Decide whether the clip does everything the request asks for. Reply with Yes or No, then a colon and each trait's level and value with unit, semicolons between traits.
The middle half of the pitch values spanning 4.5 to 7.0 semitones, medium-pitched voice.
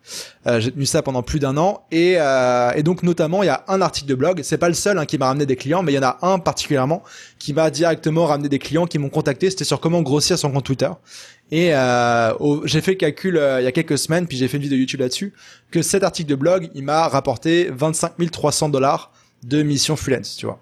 No: average, 3.8 semitones; medium, 150 Hz